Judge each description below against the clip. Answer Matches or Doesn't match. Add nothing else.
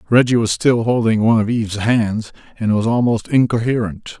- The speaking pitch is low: Matches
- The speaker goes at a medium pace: Matches